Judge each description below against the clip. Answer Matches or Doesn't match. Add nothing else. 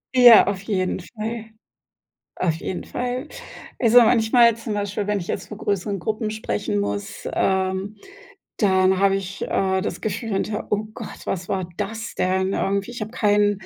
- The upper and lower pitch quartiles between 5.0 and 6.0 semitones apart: Doesn't match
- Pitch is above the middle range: Matches